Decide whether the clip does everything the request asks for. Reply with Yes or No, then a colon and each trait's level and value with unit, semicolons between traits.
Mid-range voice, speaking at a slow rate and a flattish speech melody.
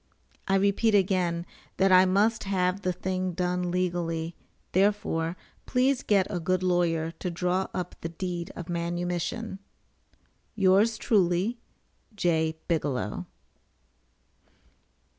Yes: medium, 180 Hz; slow, 110 wpm; narrow, 2.1 semitones